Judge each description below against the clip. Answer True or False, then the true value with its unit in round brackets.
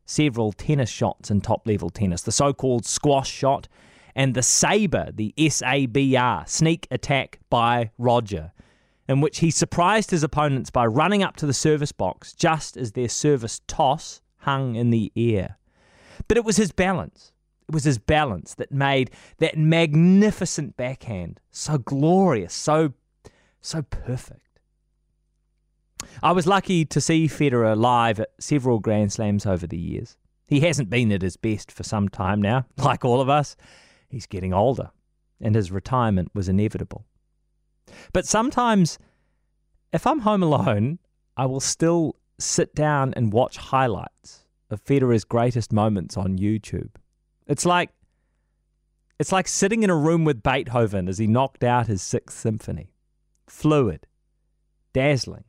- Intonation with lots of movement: True (6.1 semitones)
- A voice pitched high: False (130 Hz)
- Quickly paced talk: False (145 wpm)